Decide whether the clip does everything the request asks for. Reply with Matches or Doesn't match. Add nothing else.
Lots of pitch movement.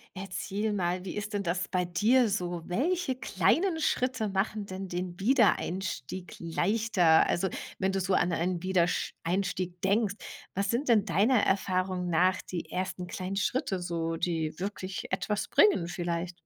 Doesn't match